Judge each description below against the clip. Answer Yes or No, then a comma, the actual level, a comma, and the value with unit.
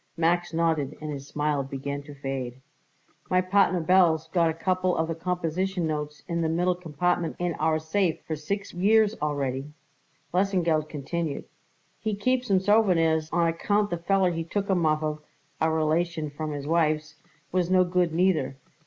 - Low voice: No, medium, 165 Hz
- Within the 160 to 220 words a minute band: Yes, average, 170 wpm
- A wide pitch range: No, average, 3.1 semitones